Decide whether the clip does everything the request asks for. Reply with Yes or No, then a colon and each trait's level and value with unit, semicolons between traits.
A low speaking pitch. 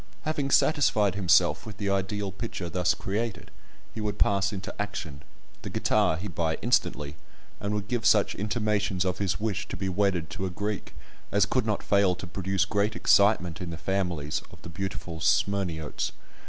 Yes: low, 100 Hz